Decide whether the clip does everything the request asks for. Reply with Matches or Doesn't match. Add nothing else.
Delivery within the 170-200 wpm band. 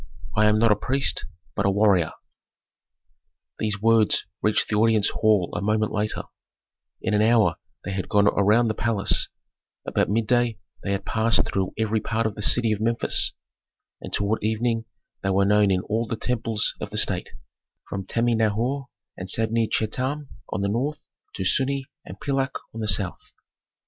Matches